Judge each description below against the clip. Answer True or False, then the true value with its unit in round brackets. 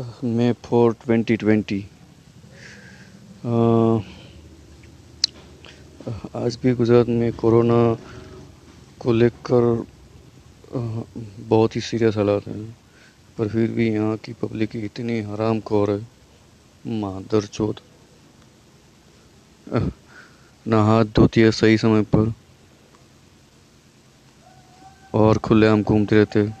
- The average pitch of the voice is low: True (110 Hz)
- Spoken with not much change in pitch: True (2.0 semitones)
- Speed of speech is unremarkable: False (85 wpm)